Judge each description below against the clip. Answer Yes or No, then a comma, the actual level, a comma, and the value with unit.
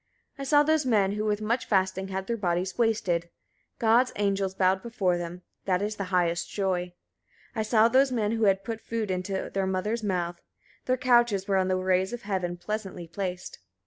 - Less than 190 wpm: No, average, 200 wpm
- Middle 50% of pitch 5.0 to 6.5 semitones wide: No, average, 3.3 semitones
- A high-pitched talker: Yes, high, 195 Hz